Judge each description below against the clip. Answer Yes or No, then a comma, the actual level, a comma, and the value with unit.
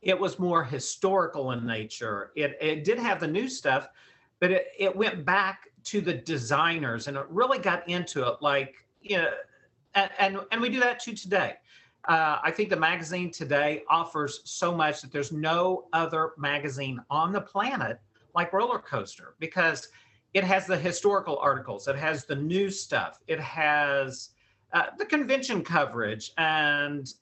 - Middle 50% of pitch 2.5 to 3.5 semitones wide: No, average, 5.1 semitones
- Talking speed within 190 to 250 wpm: No, average, 170 wpm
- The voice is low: No, medium, 160 Hz